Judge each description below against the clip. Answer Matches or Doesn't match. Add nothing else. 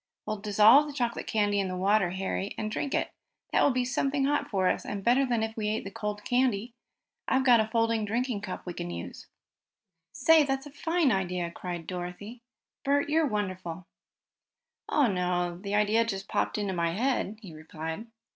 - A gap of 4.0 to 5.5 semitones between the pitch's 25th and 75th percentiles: Matches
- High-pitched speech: Matches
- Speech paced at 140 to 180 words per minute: Doesn't match